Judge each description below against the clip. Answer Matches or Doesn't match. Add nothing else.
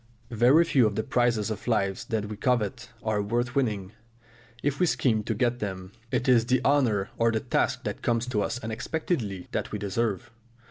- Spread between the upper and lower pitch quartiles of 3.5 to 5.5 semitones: Doesn't match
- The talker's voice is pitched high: Doesn't match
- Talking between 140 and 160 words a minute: Doesn't match